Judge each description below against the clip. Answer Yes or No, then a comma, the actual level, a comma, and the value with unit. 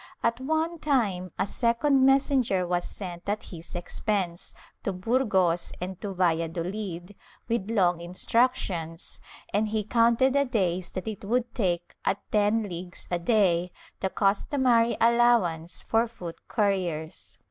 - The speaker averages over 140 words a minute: No, slow, 135 wpm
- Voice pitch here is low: No, high, 200 Hz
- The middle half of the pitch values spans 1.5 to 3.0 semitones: No, average, 4.8 semitones